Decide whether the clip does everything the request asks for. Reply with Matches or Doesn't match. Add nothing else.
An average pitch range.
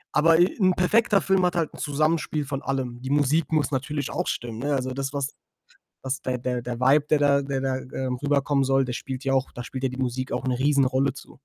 Doesn't match